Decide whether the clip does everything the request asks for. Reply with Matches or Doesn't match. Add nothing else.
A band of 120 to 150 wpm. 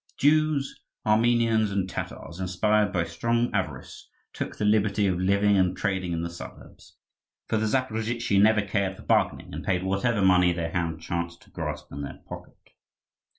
Doesn't match